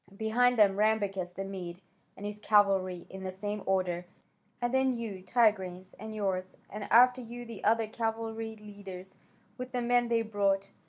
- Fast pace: No, average, 165 wpm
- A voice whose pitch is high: Yes, high, 210 Hz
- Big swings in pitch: No, average, 3.1 semitones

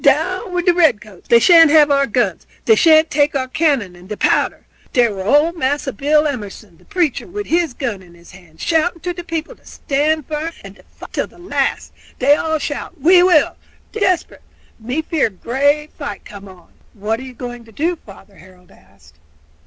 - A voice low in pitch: No, very high, 285 Hz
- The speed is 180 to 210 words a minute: Yes, fast, 205 wpm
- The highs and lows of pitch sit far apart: Yes, wide, 7.1 semitones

